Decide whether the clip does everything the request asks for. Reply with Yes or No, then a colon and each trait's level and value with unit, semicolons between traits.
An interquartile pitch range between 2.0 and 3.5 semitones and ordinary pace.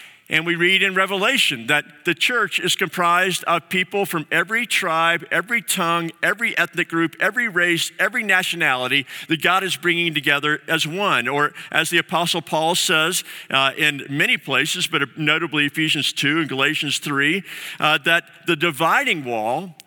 Yes: average, 2.8 semitones; average, 160 wpm